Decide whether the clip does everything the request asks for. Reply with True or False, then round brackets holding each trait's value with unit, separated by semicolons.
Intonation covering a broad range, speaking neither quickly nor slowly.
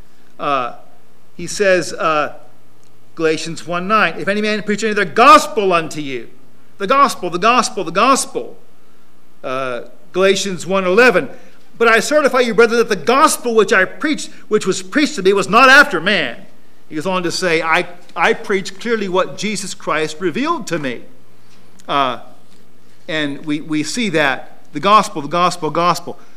True (6.2 semitones; 160 wpm)